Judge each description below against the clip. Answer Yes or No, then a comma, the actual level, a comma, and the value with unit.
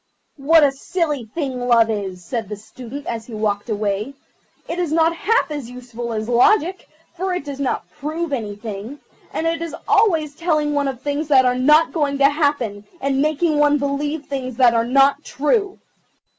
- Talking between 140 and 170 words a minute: No, average, 185 wpm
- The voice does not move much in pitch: No, average, 4.7 semitones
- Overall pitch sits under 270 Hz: No, very high, 280 Hz